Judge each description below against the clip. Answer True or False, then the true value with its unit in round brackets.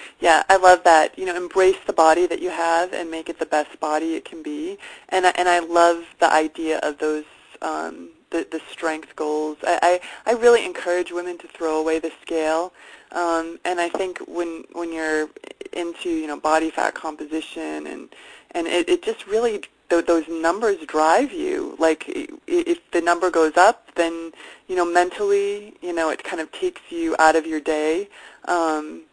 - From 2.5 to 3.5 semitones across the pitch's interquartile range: True (2.8 semitones)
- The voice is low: False (170 Hz)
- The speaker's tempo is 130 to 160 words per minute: False (185 wpm)